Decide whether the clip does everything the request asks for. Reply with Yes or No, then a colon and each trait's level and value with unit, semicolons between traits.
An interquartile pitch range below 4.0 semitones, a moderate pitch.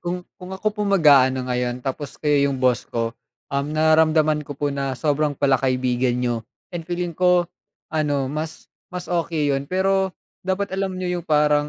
No: average, 4.7 semitones; medium, 150 Hz